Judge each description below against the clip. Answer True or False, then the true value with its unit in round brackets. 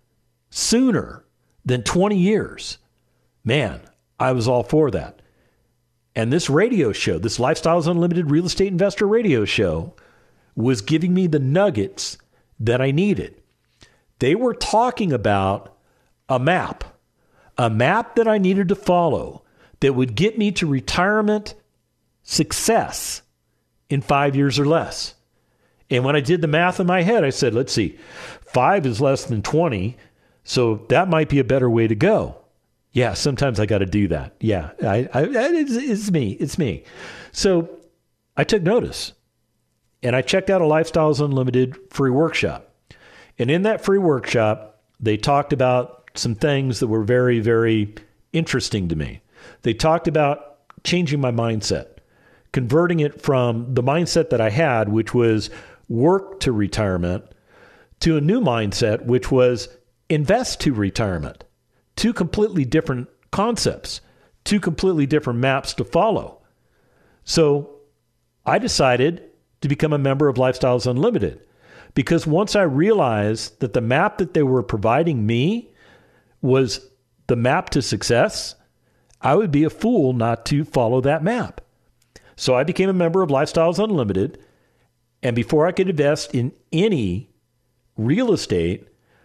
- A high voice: False (135 Hz)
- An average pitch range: False (6.3 semitones)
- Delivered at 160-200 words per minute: False (145 wpm)